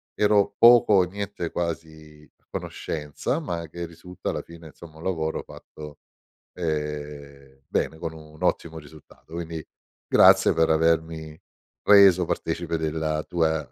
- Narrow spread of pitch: Yes, narrow, 2.0 semitones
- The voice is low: Yes, very low, 80 Hz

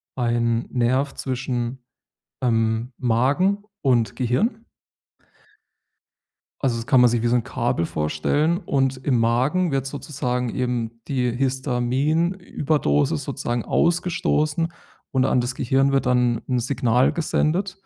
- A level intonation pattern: No, average, 3.4 semitones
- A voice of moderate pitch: No, low, 130 Hz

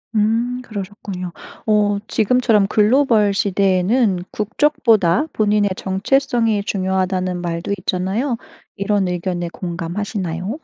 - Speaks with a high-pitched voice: Yes, high, 200 Hz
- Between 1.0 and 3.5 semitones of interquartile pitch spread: Yes, average, 3.2 semitones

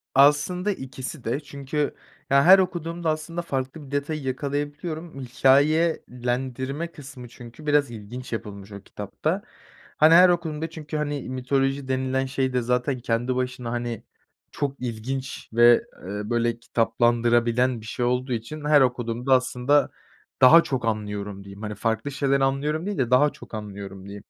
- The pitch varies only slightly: No, average, 3.7 semitones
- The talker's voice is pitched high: No, low, 130 Hz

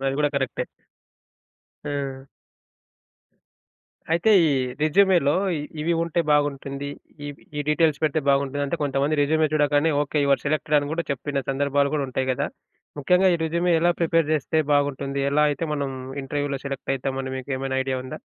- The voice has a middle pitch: Yes, medium, 145 Hz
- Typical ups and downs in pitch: No, narrow, 2.2 semitones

